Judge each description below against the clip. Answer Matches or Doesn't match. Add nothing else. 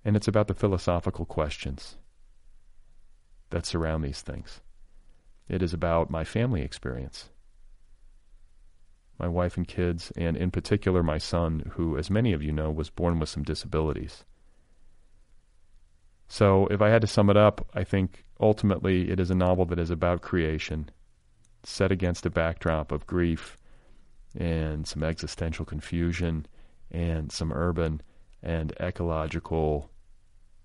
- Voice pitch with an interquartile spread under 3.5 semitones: Matches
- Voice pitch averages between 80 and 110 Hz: Matches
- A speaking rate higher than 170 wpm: Doesn't match